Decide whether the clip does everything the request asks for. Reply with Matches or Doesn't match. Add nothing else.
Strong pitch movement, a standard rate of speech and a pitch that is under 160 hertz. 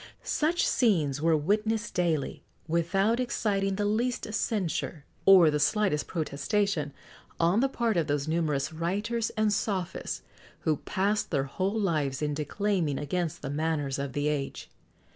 Doesn't match